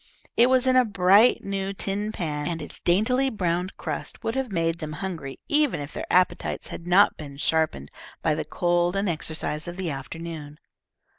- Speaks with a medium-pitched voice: Yes, medium, 175 Hz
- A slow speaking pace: No, average, 180 wpm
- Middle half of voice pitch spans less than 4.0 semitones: No, average, 4.5 semitones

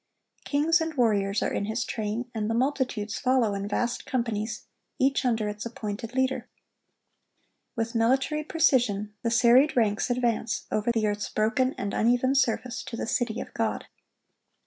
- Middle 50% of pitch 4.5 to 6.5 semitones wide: No, average, 3.3 semitones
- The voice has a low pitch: No, high, 235 Hz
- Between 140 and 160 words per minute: Yes, average, 155 wpm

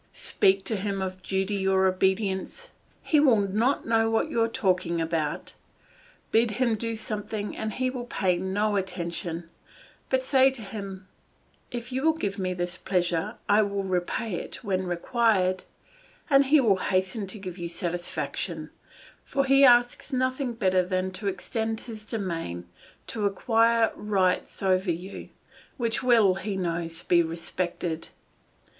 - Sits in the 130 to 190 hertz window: No, high, 200 Hz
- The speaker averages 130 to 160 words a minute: Yes, average, 150 wpm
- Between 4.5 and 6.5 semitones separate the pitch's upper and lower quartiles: No, average, 3.7 semitones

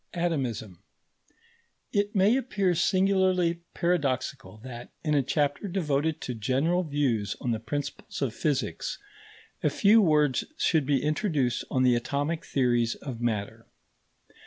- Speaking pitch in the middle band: Yes, medium, 145 Hz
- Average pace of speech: No, slow, 130 wpm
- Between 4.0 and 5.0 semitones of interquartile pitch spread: No, wide, 5.6 semitones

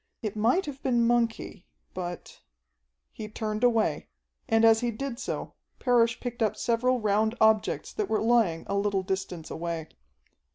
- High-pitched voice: Yes, high, 220 Hz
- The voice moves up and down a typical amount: Yes, average, 3.1 semitones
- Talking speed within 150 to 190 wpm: Yes, average, 155 wpm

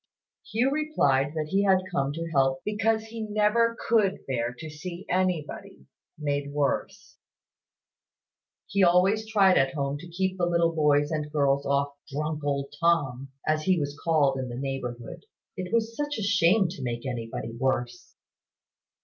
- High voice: No, medium, 155 Hz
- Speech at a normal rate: Yes, average, 160 wpm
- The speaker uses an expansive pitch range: Yes, wide, 5.7 semitones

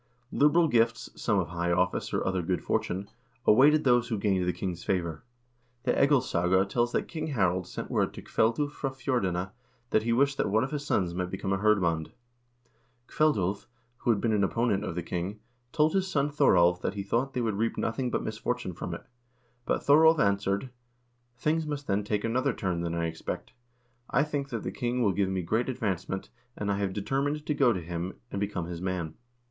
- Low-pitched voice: Yes, low, 105 Hz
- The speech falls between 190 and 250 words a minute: Yes, average, 200 wpm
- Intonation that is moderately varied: No, wide, 6.2 semitones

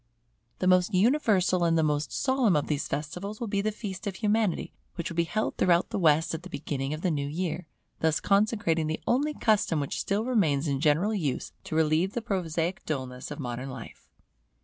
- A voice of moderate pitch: Yes, medium, 170 Hz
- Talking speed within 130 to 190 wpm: No, average, 200 wpm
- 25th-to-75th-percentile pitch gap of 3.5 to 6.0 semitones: Yes, average, 5.1 semitones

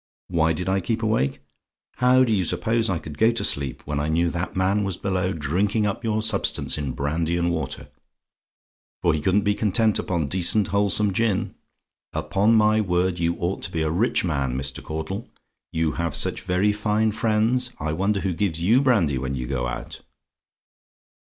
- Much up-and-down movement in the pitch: No, average, 4.9 semitones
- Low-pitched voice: Yes, very low, 95 Hz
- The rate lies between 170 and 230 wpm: Yes, average, 185 wpm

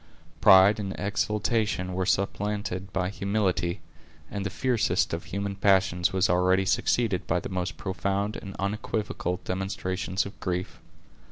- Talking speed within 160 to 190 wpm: No, slow, 135 wpm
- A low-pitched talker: Yes, very low, 95 Hz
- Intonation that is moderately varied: No, narrow, 1.7 semitones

